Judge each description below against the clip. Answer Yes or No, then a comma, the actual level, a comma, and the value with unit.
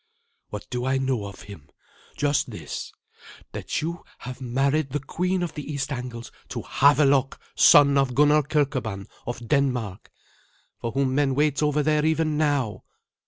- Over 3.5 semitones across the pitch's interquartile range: No, average, 3.2 semitones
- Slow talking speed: No, average, 155 wpm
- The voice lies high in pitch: No, medium, 140 Hz